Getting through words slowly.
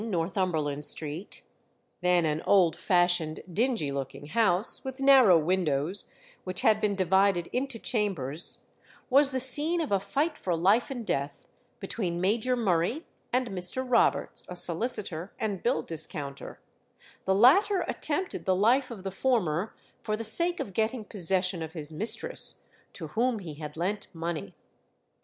No: average, 150 wpm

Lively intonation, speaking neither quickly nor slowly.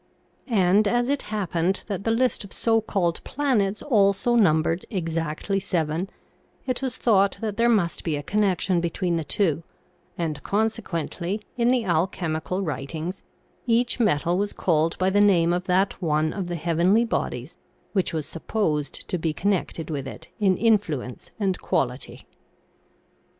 No: average, 4.3 semitones; average, 155 wpm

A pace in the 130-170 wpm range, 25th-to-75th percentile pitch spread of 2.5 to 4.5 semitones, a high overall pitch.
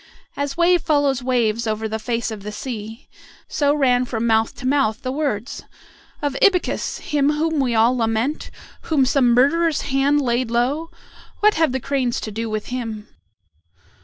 Yes: average, 165 wpm; average, 4.1 semitones; very high, 255 Hz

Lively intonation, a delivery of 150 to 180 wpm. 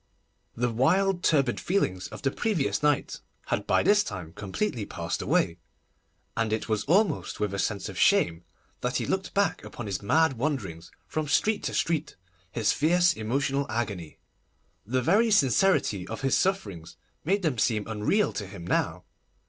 Yes: wide, 8.4 semitones; average, 165 wpm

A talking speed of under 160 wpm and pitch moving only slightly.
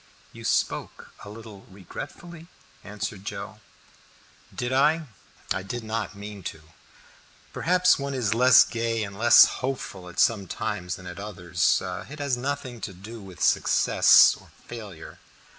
No: average, 140 wpm; average, 4.8 semitones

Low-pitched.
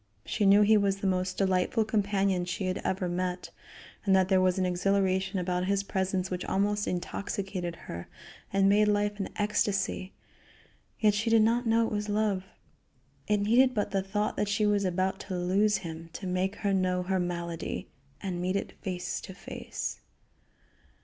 No: high, 195 Hz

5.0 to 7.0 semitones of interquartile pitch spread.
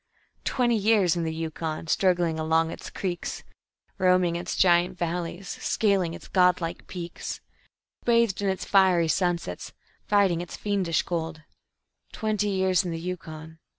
No: narrow, 2.6 semitones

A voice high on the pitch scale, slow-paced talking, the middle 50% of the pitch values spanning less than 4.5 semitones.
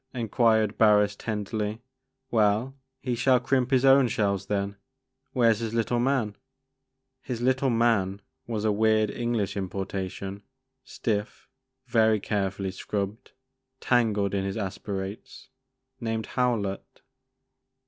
No: low, 110 Hz; slow, 130 wpm; average, 3.1 semitones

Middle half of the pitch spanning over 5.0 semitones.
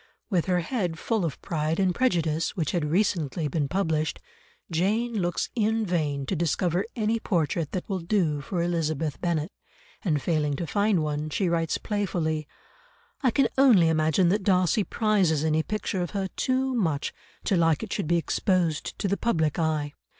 No: average, 4.3 semitones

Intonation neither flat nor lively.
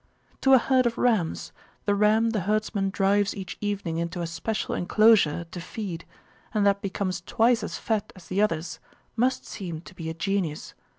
Yes: average, 3.8 semitones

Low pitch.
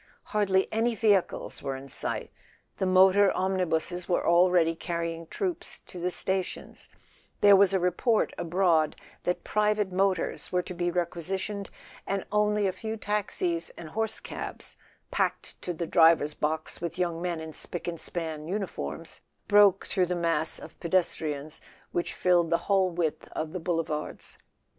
No: medium, 180 Hz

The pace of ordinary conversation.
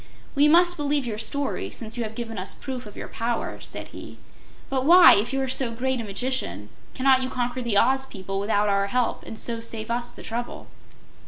No: fast, 215 wpm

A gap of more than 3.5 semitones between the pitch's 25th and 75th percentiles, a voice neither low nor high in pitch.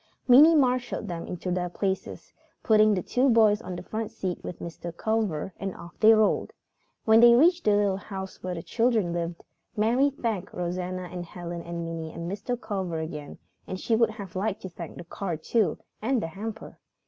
No: average, 4.4 semitones; high, 195 Hz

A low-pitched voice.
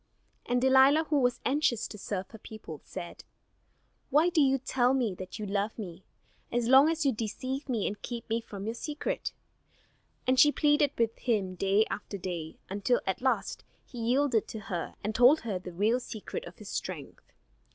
No: high, 235 Hz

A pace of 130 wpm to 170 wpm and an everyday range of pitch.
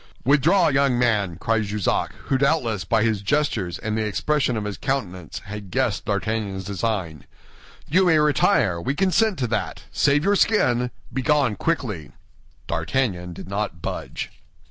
No: average, 145 wpm; wide, 6.0 semitones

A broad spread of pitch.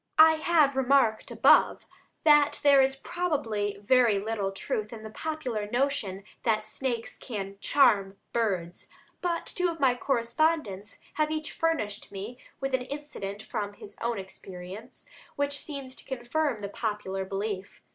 Yes: wide, 5.7 semitones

